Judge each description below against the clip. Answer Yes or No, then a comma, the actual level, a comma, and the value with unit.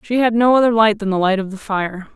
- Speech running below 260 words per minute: No, fast, 305 wpm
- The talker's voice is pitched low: No, high, 210 Hz